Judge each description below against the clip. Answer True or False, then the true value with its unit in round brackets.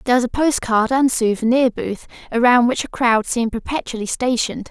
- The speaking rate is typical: True (180 wpm)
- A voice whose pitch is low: False (240 Hz)